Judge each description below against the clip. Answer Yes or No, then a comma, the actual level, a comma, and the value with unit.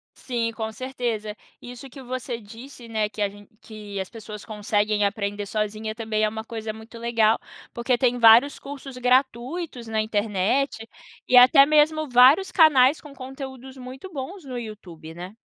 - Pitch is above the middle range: Yes, high, 235 Hz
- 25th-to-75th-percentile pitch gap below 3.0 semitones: No, average, 3.5 semitones